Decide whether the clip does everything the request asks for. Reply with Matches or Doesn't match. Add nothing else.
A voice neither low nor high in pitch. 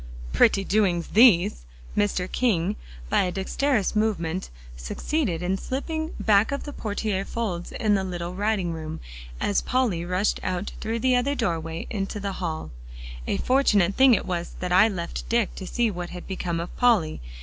Doesn't match